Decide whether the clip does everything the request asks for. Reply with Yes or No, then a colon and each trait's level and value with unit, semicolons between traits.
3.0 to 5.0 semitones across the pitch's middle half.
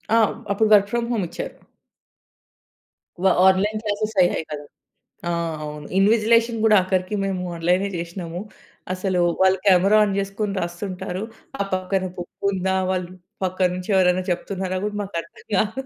No: narrow, 2.4 semitones